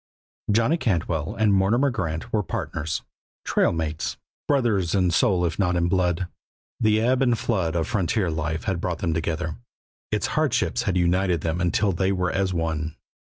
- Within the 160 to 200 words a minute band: Yes, average, 170 wpm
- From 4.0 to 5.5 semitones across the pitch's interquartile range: Yes, average, 4.5 semitones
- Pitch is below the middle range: Yes, very low, 90 Hz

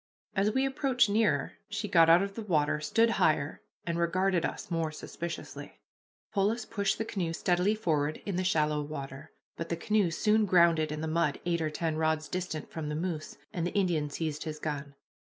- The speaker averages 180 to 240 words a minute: Yes, average, 190 wpm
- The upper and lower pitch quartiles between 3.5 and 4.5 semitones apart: Yes, average, 4.2 semitones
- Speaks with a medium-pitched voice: Yes, medium, 170 Hz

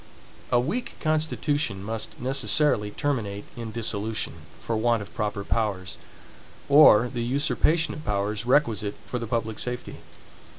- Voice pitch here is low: Yes, low, 115 Hz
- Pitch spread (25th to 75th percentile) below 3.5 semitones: No, average, 5.0 semitones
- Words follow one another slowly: Yes, slow, 130 wpm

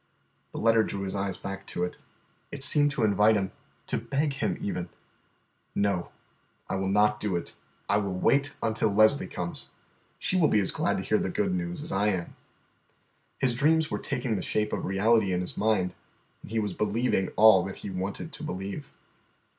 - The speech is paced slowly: No, average, 195 wpm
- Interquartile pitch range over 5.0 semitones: No, average, 4.3 semitones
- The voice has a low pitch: Yes, low, 105 Hz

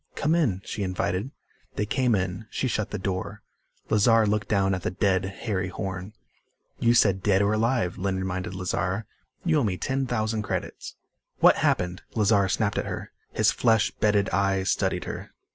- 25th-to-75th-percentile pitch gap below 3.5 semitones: Yes, average, 2.8 semitones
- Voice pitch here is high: No, low, 100 Hz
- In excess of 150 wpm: Yes, average, 175 wpm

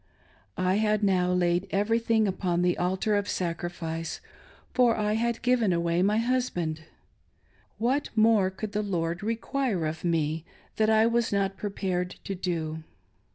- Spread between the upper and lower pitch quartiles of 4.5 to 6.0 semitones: No, average, 4.0 semitones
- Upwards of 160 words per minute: No, average, 145 wpm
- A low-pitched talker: No, high, 195 Hz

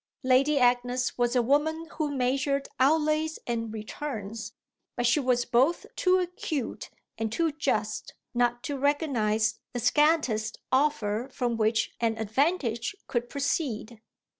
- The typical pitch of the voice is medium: No, very high, 255 Hz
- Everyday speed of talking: No, slow, 130 wpm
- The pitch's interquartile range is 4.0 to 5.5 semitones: Yes, average, 4.4 semitones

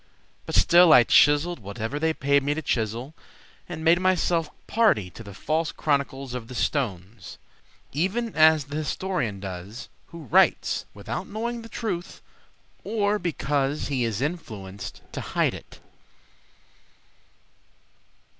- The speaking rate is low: Yes, slow, 130 wpm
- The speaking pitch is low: No, medium, 145 Hz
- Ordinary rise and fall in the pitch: No, wide, 6.9 semitones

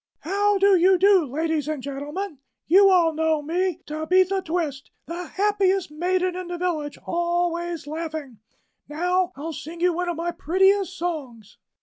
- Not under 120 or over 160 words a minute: Yes, average, 150 wpm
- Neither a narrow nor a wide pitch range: Yes, average, 3.1 semitones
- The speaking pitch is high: Yes, very high, 345 Hz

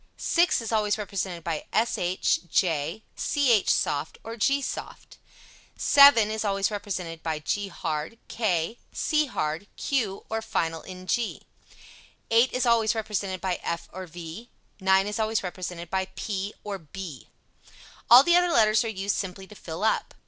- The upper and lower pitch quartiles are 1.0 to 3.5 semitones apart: No, average, 4.1 semitones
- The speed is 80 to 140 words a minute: No, average, 155 wpm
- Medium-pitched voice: No, high, 200 Hz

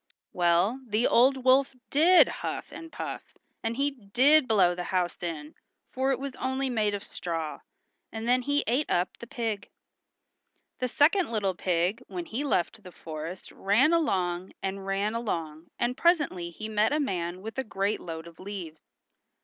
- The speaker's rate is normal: Yes, average, 170 wpm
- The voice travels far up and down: Yes, wide, 6.7 semitones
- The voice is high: Yes, high, 215 Hz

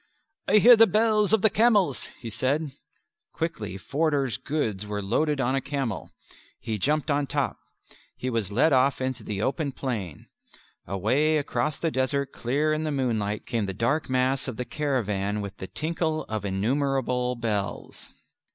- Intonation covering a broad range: Yes, wide, 5.8 semitones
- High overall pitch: No, low, 130 Hz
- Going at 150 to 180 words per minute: Yes, average, 160 wpm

